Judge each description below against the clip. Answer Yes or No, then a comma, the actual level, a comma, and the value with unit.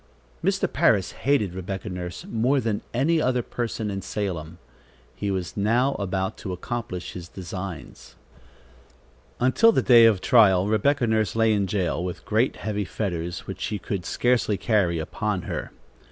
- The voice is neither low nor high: No, low, 105 Hz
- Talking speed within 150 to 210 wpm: Yes, average, 155 wpm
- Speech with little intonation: No, average, 4.3 semitones